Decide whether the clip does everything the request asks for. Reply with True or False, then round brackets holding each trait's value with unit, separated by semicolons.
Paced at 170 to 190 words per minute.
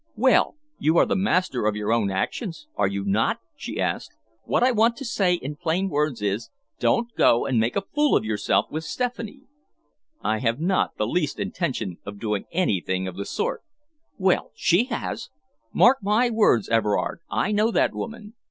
True (180 wpm)